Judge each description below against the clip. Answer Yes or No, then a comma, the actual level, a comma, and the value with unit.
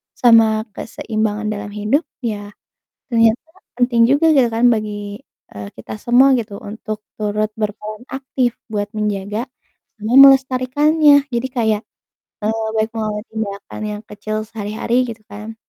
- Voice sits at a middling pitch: No, high, 220 Hz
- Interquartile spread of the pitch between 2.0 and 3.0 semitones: Yes, narrow, 2.6 semitones